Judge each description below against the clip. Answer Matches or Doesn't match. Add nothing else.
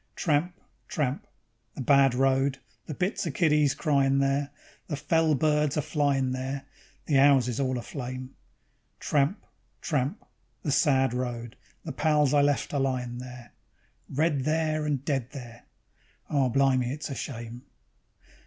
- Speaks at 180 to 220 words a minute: Doesn't match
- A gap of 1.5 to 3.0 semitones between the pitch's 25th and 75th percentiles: Matches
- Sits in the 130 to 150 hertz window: Matches